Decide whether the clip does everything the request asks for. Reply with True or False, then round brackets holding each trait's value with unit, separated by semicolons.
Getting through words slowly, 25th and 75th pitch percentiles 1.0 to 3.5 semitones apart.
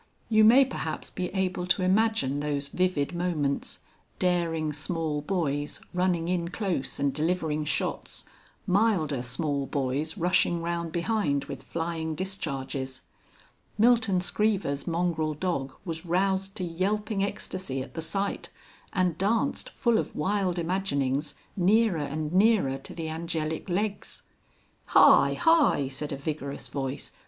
False (130 wpm; 4.5 semitones)